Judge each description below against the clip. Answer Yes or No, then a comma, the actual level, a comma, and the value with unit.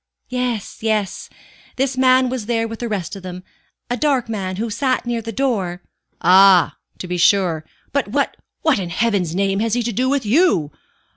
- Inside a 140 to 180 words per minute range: No, average, 195 wpm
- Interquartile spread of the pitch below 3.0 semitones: No, average, 5.0 semitones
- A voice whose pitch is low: No, high, 225 Hz